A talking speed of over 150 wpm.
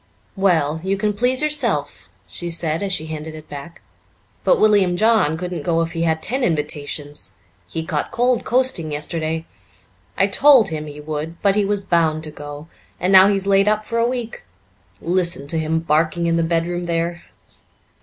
Yes: average, 180 wpm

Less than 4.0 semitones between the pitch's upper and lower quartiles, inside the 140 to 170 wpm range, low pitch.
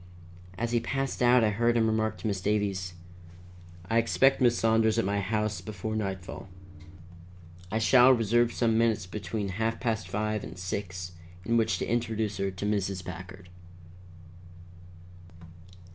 Yes: average, 2.8 semitones; average, 145 wpm; low, 110 Hz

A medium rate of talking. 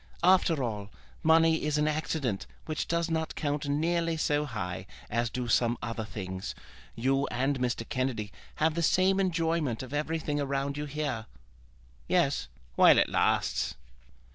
Yes: average, 145 wpm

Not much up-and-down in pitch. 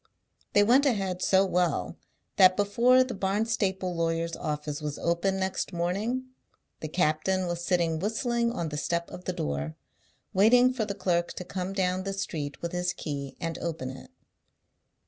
No: average, 3.4 semitones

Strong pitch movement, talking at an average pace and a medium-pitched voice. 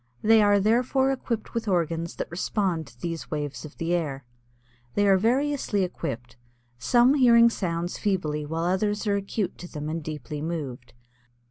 Yes: wide, 5.9 semitones; average, 165 wpm; medium, 180 Hz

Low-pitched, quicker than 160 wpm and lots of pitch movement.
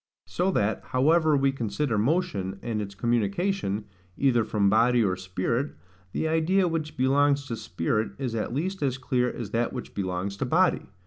Yes: low, 125 Hz; average, 170 wpm; wide, 6.1 semitones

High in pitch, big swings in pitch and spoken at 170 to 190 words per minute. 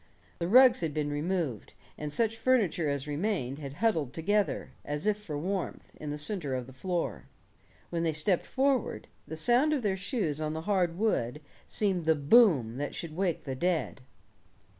No: medium, 165 Hz; wide, 5.9 semitones; average, 180 wpm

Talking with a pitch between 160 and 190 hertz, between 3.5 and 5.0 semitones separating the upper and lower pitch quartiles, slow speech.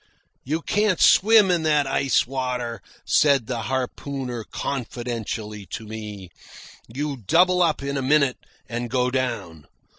No: low, 130 Hz; average, 4.1 semitones; slow, 130 wpm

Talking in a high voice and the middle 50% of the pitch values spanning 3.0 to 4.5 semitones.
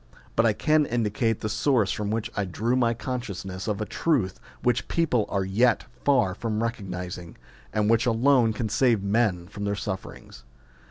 No: low, 110 Hz; average, 3.4 semitones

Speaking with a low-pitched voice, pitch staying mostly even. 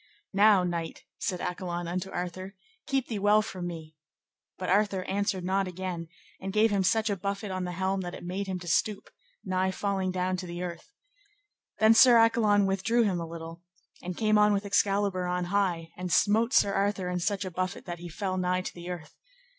No: high, 190 Hz; narrow, 2.3 semitones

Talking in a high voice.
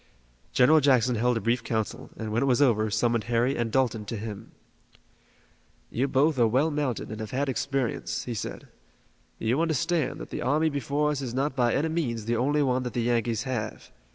No: low, 125 Hz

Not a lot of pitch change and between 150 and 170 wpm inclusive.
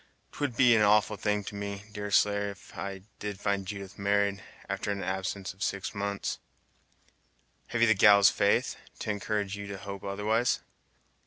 Yes: narrow, 0.9 semitones; average, 165 wpm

